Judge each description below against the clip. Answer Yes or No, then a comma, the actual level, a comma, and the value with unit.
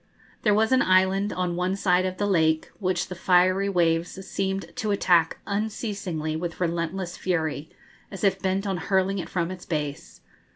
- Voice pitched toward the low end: No, medium, 185 Hz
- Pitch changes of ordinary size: No, narrow, 2.2 semitones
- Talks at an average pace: Yes, average, 170 wpm